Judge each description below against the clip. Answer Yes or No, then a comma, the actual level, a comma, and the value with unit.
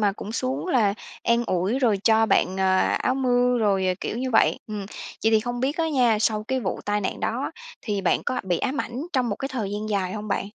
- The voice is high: Yes, high, 220 Hz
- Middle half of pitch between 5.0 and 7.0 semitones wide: No, average, 3.9 semitones